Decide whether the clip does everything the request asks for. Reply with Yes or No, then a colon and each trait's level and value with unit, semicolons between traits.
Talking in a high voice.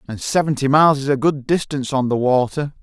No: medium, 140 Hz